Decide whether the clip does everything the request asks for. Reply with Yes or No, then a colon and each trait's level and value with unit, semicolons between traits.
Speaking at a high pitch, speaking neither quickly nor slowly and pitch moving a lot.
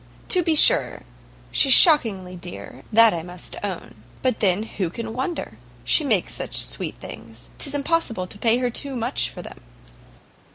Yes: high, 225 Hz; average, 165 wpm; wide, 6.9 semitones